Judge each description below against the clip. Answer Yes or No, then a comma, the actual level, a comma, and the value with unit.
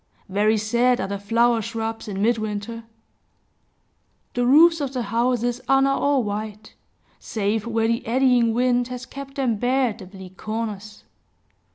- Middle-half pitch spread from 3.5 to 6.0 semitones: No, average, 2.8 semitones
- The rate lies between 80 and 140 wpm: No, average, 155 wpm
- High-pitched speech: Yes, high, 230 Hz